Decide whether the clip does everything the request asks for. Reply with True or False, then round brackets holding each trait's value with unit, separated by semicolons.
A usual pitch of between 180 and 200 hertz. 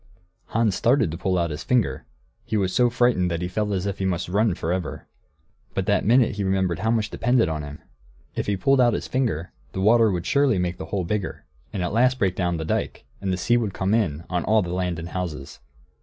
False (95 Hz)